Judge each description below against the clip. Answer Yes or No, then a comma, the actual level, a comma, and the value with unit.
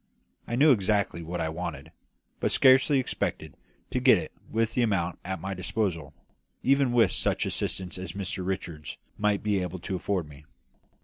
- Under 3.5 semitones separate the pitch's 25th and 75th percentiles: No, average, 4.3 semitones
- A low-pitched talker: Yes, very low, 95 Hz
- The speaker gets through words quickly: No, average, 170 wpm